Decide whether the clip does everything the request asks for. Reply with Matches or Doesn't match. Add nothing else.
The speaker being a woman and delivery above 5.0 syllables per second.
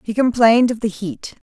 Matches